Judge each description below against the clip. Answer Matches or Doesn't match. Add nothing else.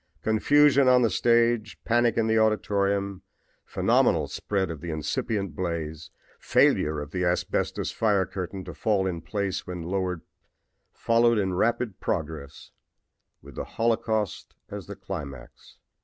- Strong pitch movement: Doesn't match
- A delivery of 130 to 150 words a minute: Matches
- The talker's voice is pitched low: Matches